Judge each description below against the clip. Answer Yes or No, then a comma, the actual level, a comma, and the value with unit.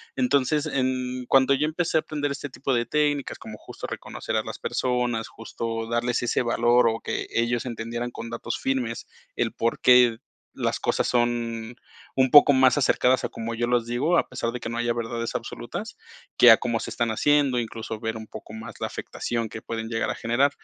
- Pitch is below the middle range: Yes, low, 120 Hz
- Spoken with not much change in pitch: Yes, narrow, 2.2 semitones